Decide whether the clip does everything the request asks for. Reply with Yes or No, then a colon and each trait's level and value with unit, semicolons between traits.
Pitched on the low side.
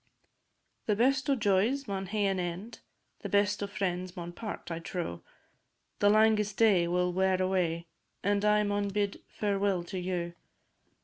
No: high, 195 Hz